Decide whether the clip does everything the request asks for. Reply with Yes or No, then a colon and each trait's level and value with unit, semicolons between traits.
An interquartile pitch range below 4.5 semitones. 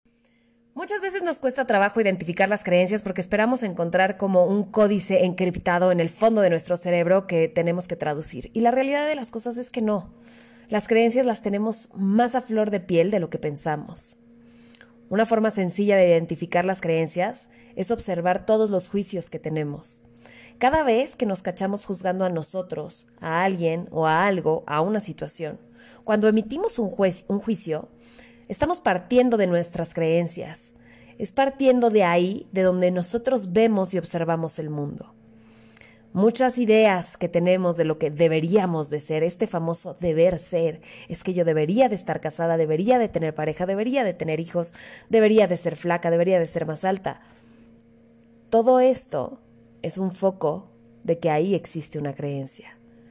No: average, 5.2 semitones